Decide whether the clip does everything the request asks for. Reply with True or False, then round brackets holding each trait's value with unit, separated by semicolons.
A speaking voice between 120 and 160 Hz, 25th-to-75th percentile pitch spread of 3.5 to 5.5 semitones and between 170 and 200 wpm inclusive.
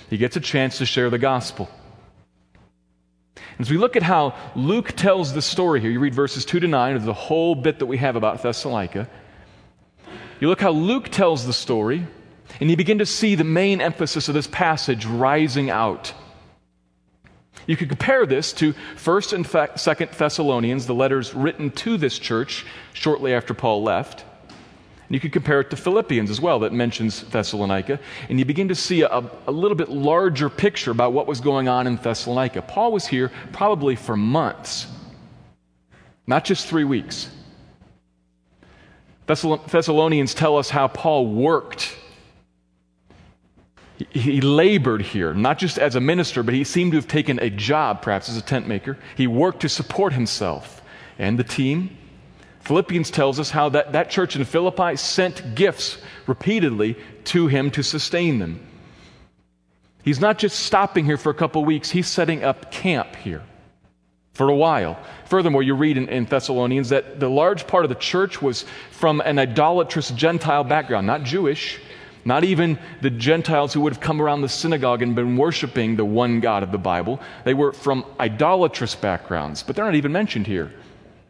True (140 Hz; 5.1 semitones; 175 wpm)